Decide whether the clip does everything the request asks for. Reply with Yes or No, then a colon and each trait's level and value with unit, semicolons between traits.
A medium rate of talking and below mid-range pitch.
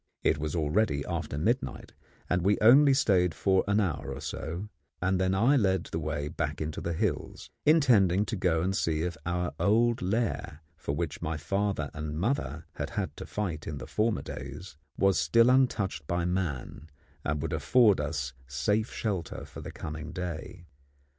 Yes: average, 175 wpm; very low, 90 Hz